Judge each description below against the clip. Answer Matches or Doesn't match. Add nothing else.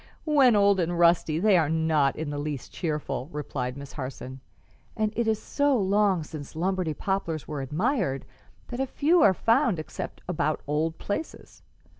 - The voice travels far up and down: Matches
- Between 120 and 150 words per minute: Doesn't match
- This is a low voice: Doesn't match